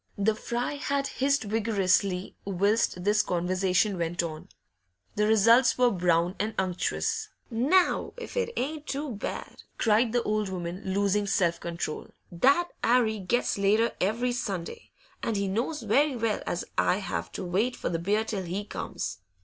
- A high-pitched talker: Yes, high, 210 Hz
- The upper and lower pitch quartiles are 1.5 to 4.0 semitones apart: No, average, 4.5 semitones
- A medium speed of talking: Yes, average, 155 wpm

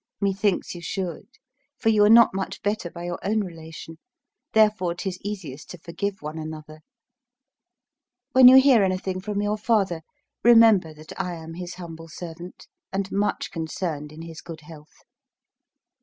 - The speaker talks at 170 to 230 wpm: No, average, 155 wpm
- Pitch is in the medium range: Yes, medium, 180 Hz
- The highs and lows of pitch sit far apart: No, average, 4.0 semitones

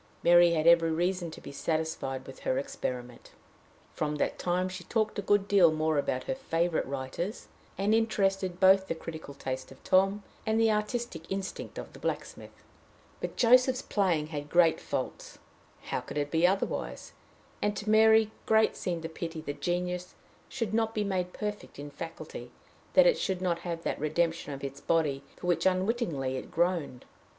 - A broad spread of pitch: No, average, 4.6 semitones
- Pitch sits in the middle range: Yes, medium, 175 Hz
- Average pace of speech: Yes, average, 175 wpm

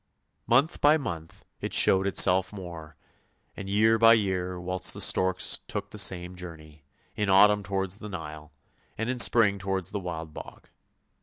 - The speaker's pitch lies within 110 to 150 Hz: No, very low, 95 Hz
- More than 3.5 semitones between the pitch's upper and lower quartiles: No, average, 2.9 semitones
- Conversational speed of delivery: Yes, average, 160 wpm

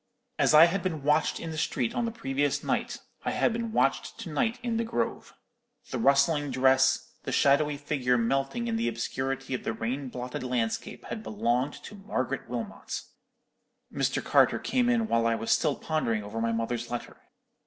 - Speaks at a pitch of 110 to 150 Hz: Yes, medium, 140 Hz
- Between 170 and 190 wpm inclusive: Yes, average, 185 wpm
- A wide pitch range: Yes, wide, 6.9 semitones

